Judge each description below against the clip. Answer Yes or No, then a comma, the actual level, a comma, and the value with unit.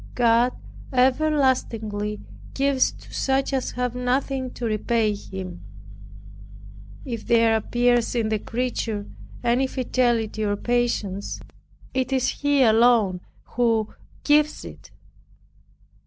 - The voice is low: No, high, 240 Hz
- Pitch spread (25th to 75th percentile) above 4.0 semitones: No, average, 3.0 semitones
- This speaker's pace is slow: Yes, slow, 105 wpm